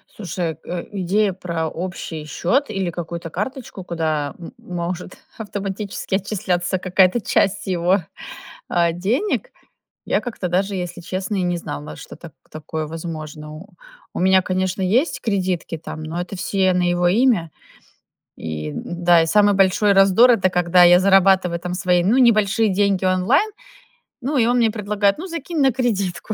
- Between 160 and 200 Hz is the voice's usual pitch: Yes, medium, 185 Hz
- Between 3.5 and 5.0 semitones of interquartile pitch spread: No, average, 3.1 semitones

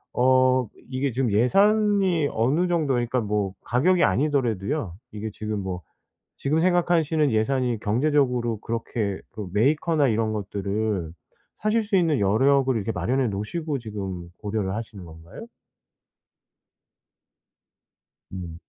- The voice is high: No, low, 120 Hz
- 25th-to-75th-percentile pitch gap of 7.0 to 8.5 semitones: No, wide, 6.1 semitones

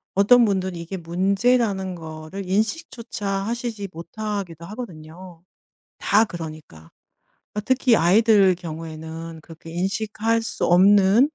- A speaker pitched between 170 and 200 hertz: Yes, high, 190 Hz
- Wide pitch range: No, average, 4.6 semitones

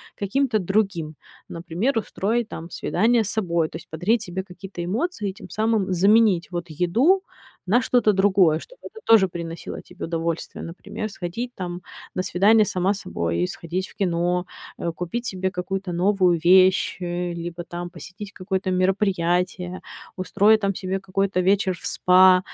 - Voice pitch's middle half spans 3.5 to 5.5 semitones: No, average, 2.9 semitones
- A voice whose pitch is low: No, medium, 185 Hz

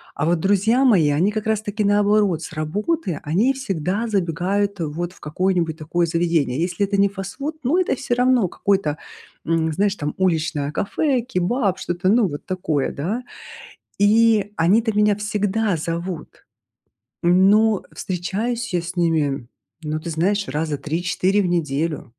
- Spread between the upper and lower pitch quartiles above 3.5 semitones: Yes, average, 4.2 semitones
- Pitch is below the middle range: No, medium, 185 Hz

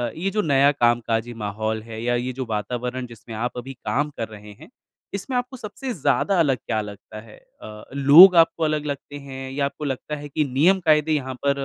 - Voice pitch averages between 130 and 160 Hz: Yes, low, 135 Hz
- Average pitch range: Yes, average, 4.8 semitones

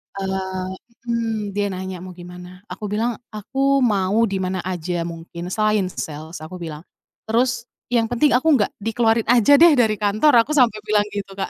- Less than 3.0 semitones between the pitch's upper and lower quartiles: No, average, 4.0 semitones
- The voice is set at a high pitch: Yes, high, 205 Hz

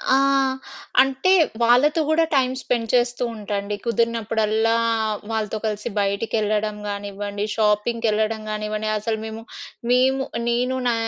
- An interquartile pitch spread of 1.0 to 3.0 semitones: Yes, narrow, 2.4 semitones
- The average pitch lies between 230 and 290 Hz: No, high, 220 Hz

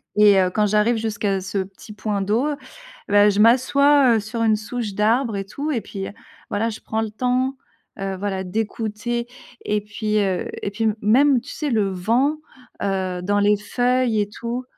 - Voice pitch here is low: No, high, 215 Hz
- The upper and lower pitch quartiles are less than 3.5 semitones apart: Yes, average, 2.8 semitones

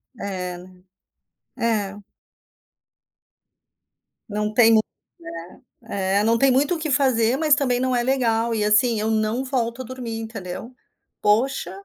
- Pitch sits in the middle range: No, high, 230 Hz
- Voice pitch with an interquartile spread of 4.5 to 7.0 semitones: No, average, 3.3 semitones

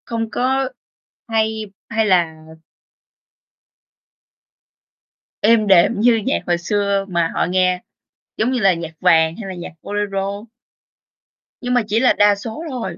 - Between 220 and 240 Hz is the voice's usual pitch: No, high, 205 Hz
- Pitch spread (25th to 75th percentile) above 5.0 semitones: No, average, 3.9 semitones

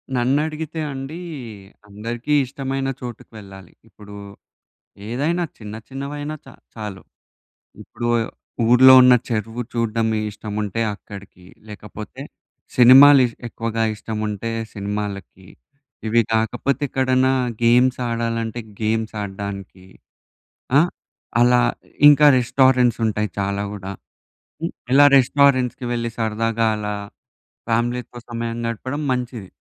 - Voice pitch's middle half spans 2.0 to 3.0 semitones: No, average, 3.4 semitones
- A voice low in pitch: Yes, low, 115 Hz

